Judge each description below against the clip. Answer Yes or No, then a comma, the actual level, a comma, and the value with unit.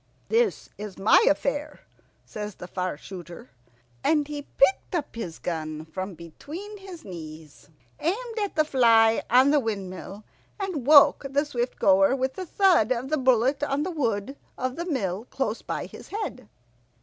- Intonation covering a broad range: Yes, wide, 7.6 semitones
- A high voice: Yes, very high, 255 Hz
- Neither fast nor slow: Yes, average, 160 wpm